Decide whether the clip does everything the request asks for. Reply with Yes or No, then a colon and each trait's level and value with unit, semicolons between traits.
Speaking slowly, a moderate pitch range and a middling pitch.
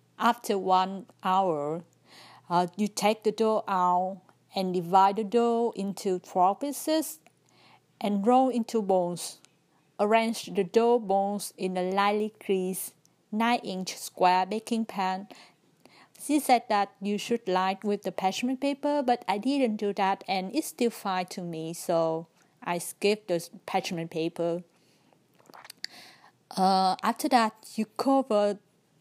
No: slow, 135 wpm; average, 3.5 semitones; high, 200 Hz